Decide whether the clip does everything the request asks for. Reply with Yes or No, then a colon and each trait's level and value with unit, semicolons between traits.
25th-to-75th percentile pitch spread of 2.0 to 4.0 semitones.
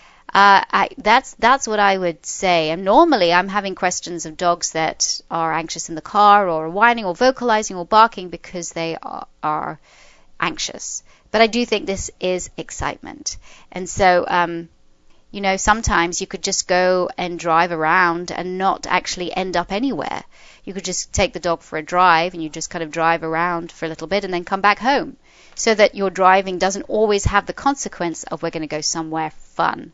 Yes: average, 3.2 semitones